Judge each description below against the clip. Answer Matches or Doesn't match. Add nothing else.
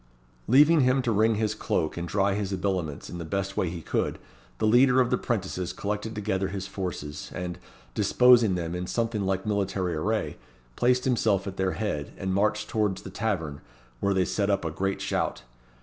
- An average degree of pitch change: Matches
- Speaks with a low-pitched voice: Matches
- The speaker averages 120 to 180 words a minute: Doesn't match